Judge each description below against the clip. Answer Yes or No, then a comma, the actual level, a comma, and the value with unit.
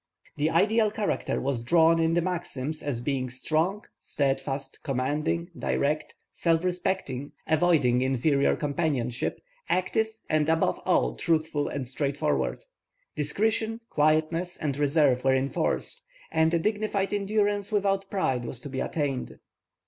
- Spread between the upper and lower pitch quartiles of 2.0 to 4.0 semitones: No, average, 4.8 semitones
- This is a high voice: No, medium, 155 Hz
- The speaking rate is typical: No, slow, 125 wpm